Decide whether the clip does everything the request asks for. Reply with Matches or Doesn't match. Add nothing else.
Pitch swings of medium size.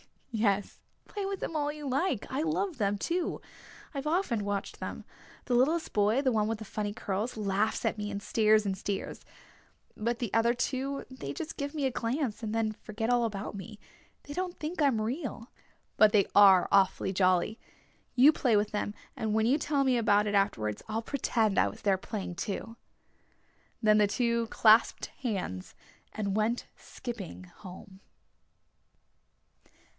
Matches